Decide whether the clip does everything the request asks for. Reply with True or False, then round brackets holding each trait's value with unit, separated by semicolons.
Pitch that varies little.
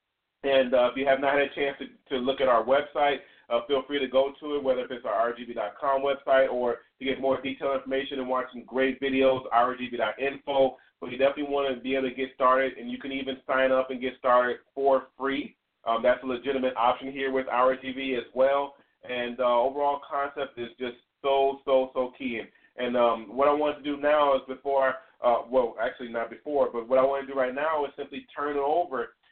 True (1.6 semitones)